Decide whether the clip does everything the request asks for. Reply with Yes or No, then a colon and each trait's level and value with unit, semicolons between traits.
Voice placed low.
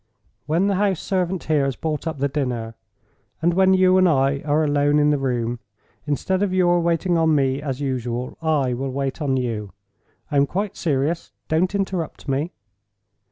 No: medium, 150 Hz